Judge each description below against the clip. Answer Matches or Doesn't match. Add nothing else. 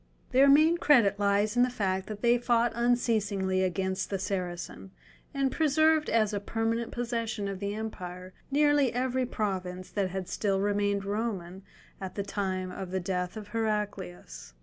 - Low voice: Doesn't match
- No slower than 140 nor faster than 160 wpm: Matches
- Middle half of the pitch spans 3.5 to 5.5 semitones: Matches